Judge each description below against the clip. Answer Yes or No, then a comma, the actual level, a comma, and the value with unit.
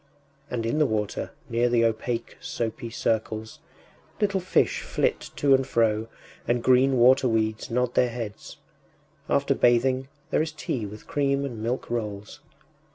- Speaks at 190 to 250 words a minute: No, average, 150 wpm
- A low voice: Yes, low, 120 Hz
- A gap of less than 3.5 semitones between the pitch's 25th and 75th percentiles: Yes, average, 2.9 semitones